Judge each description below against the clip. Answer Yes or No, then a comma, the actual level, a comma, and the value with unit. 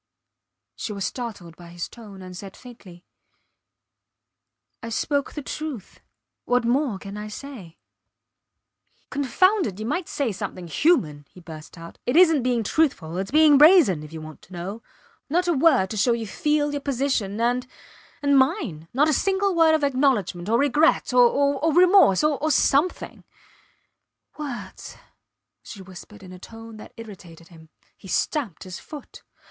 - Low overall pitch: No, high, 235 Hz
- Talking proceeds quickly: No, average, 155 wpm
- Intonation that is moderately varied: No, wide, 7.6 semitones